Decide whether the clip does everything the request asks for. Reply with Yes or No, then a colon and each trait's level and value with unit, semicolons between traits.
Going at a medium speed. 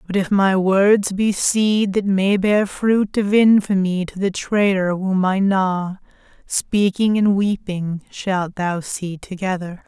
Yes: average, 150 wpm